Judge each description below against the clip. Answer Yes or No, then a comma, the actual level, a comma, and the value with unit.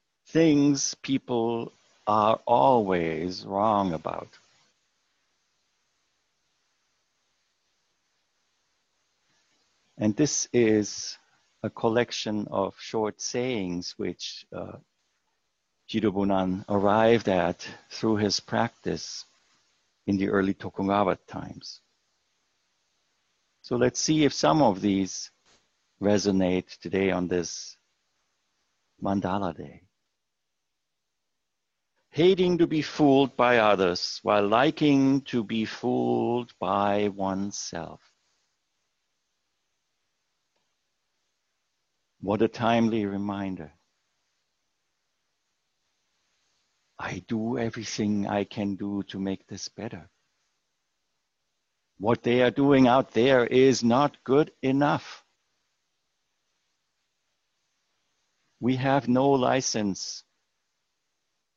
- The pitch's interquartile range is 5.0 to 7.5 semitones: No, average, 4.2 semitones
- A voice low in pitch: Yes, low, 105 Hz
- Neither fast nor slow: No, slow, 80 wpm